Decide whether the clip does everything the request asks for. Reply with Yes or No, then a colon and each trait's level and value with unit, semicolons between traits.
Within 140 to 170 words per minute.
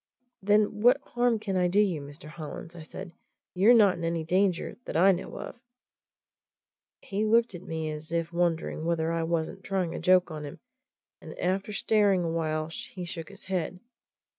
No: average, 185 wpm